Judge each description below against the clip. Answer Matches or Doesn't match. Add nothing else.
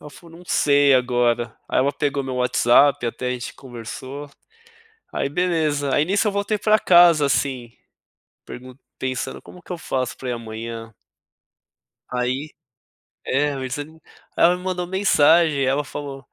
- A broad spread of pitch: Doesn't match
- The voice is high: Doesn't match